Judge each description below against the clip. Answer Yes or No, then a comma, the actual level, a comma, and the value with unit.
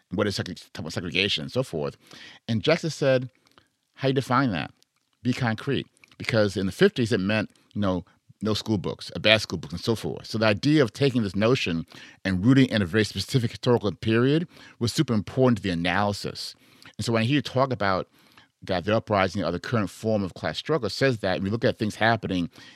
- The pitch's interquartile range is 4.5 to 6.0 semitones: Yes, average, 4.8 semitones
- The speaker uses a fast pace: Yes, fast, 210 wpm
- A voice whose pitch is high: No, low, 110 Hz